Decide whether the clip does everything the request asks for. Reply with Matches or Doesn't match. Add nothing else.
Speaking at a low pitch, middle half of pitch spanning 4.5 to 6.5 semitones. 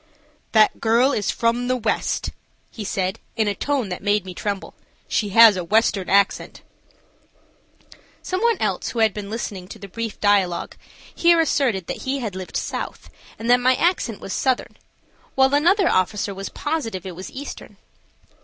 Doesn't match